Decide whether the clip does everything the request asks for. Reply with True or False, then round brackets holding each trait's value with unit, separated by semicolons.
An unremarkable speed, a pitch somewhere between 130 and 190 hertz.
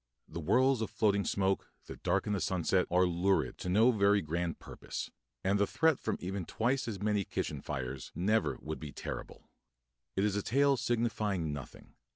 False (180 wpm; 100 Hz)